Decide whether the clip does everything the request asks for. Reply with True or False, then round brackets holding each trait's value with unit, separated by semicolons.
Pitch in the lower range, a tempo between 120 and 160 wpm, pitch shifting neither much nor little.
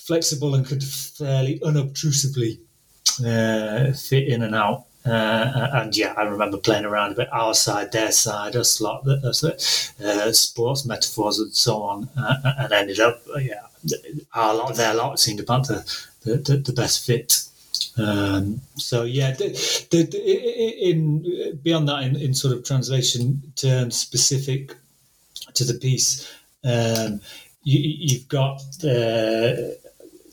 True (130 Hz; 145 wpm; 4.1 semitones)